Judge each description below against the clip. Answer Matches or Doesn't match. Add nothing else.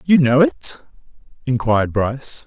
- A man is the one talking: Matches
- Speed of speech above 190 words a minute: Doesn't match